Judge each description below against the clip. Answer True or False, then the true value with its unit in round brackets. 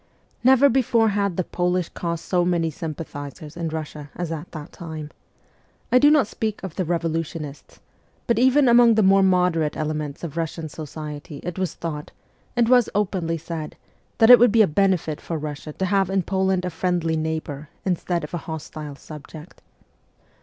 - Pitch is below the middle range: False (170 Hz)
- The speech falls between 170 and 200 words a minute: True (175 wpm)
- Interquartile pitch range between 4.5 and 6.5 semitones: False (3.9 semitones)